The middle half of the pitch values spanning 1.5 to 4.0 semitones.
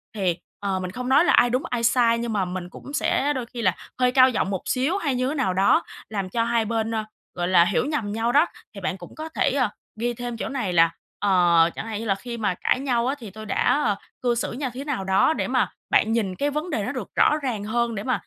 No: average, 4.6 semitones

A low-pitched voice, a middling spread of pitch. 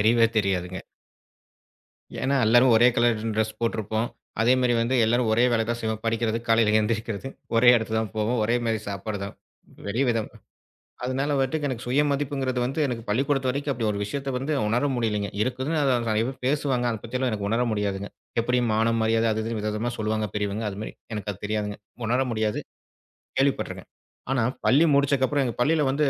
Yes: low, 115 Hz; average, 3.1 semitones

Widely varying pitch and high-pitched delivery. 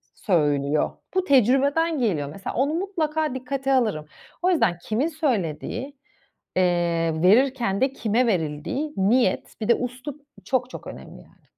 Yes: wide, 7.5 semitones; high, 245 Hz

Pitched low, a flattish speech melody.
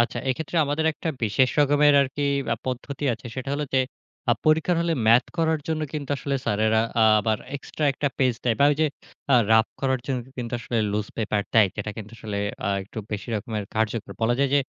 No: low, 125 Hz; average, 4.7 semitones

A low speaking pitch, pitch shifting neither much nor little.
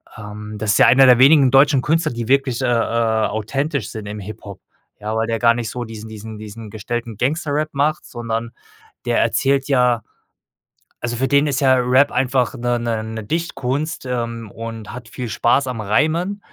Yes: low, 120 Hz; average, 3.4 semitones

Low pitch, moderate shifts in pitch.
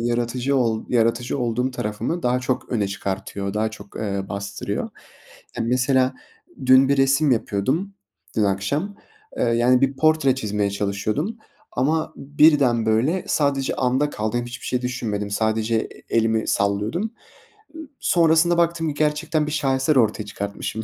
Yes: low, 125 Hz; average, 5.0 semitones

